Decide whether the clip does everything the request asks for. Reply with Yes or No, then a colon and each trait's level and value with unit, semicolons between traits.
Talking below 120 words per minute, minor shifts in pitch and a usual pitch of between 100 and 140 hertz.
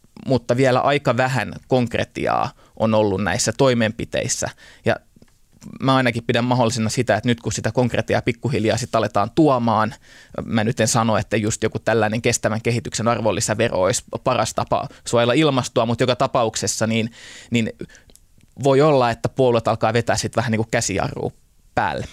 No: fast, 155 wpm; narrow, 2.2 semitones; low, 115 Hz